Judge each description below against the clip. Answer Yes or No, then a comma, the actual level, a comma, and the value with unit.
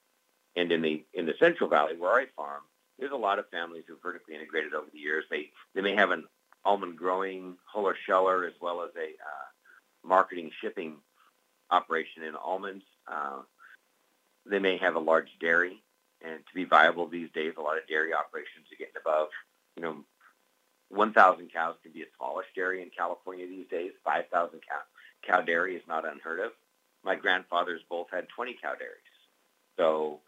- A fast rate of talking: No, average, 180 wpm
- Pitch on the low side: Yes, very low, 90 Hz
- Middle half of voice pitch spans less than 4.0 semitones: Yes, narrow, 2.6 semitones